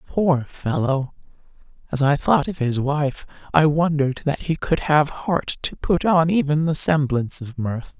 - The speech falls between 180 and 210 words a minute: No, average, 165 wpm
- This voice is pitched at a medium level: Yes, medium, 155 Hz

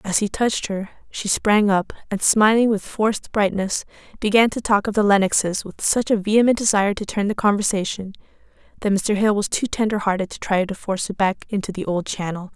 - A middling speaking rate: No, fast, 210 wpm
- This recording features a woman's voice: Yes, female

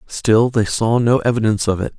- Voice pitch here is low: Yes, low, 115 Hz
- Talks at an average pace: No, fast, 210 wpm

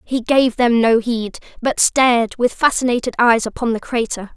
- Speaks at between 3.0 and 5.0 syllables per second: Yes, 4.8 syllables/s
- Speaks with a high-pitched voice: Yes, high, 240 Hz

